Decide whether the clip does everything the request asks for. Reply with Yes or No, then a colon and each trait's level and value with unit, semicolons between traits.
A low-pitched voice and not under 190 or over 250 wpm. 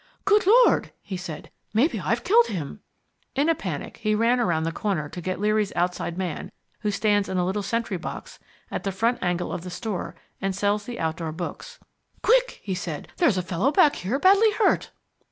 No: high, 200 Hz; average, 195 wpm